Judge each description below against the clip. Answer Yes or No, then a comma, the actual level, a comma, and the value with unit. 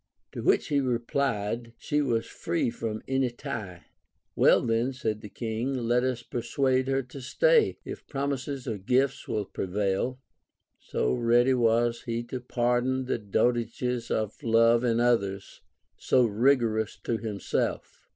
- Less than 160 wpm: Yes, average, 145 wpm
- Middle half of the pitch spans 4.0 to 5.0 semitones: No, narrow, 2.5 semitones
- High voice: No, low, 120 Hz